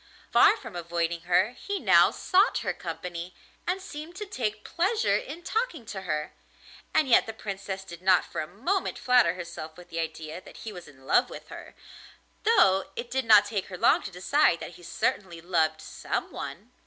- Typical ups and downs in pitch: No, wide, 7.5 semitones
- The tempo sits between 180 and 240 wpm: Yes, average, 190 wpm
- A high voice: Yes, high, 195 Hz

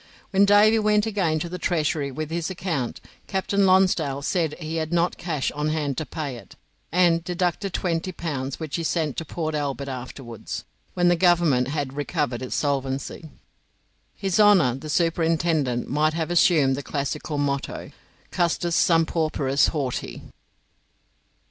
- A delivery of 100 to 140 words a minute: No, average, 150 wpm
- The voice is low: No, medium, 160 Hz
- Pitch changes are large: No, average, 3.7 semitones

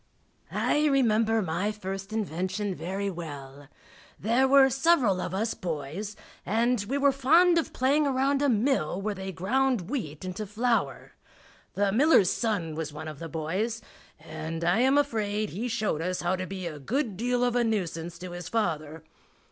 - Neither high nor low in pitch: No, high, 205 Hz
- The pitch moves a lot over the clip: Yes, wide, 6.1 semitones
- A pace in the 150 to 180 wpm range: Yes, average, 170 wpm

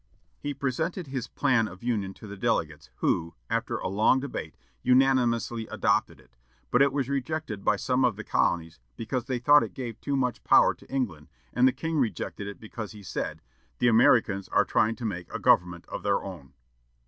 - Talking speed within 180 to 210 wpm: Yes, average, 195 wpm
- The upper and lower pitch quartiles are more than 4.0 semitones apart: Yes, average, 4.9 semitones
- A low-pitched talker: Yes, low, 120 Hz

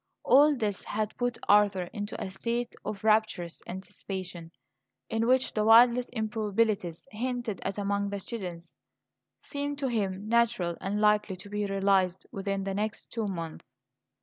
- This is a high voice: Yes, high, 210 Hz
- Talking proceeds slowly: No, average, 150 wpm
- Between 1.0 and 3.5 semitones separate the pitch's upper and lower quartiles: Yes, average, 3.0 semitones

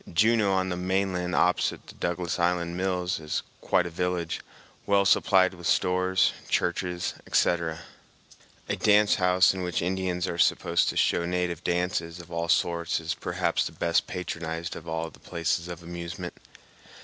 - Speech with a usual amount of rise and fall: No, narrow, 1.4 semitones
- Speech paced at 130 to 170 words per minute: Yes, average, 160 wpm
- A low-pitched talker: Yes, very low, 90 Hz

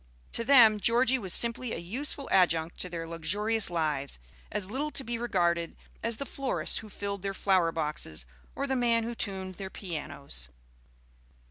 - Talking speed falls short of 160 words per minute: No, average, 165 wpm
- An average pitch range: No, wide, 5.8 semitones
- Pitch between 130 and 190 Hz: No, high, 200 Hz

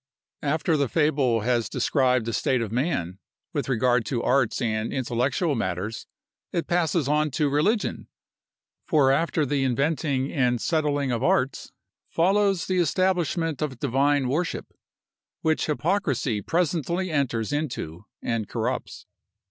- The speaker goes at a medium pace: No, slow, 130 wpm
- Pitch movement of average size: Yes, average, 4.6 semitones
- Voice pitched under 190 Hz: Yes, medium, 140 Hz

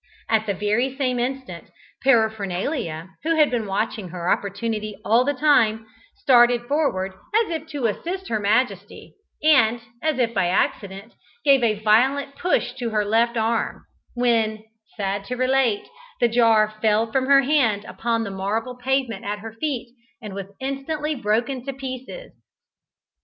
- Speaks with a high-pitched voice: Yes, high, 235 Hz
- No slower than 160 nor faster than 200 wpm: No, average, 150 wpm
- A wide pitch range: No, average, 4.0 semitones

